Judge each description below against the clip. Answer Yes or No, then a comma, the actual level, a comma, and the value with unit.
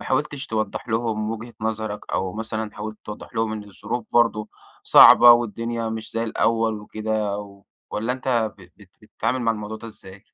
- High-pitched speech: No, low, 110 Hz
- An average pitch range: No, narrow, 1.3 semitones